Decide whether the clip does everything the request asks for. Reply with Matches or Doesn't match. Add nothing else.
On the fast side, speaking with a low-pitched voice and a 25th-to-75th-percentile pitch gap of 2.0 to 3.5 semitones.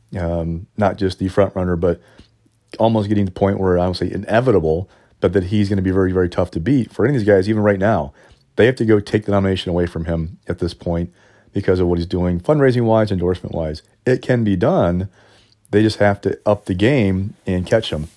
Matches